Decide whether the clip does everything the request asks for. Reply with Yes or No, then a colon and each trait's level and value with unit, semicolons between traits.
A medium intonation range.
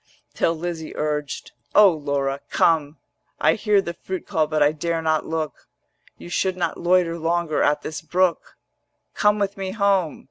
Yes: average, 3.2 semitones